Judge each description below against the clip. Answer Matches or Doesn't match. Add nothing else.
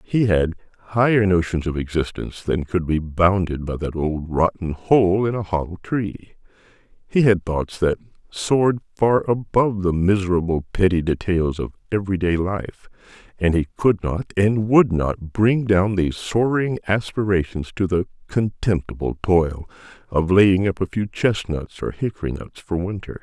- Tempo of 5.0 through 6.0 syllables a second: Doesn't match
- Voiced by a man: Matches